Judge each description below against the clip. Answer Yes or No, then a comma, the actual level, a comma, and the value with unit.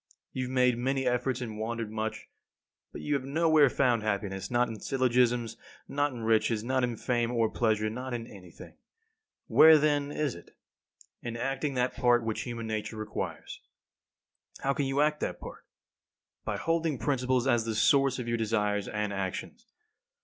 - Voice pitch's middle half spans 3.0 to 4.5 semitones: Yes, average, 3.4 semitones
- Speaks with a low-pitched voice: Yes, low, 120 Hz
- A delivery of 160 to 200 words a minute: Yes, average, 170 wpm